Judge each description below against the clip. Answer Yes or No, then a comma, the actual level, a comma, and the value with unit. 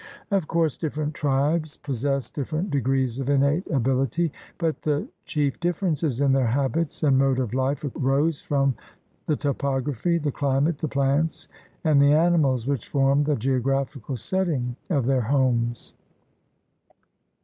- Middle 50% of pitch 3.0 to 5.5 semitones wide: No, narrow, 2.5 semitones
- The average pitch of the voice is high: No, medium, 140 Hz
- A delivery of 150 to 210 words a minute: No, average, 140 wpm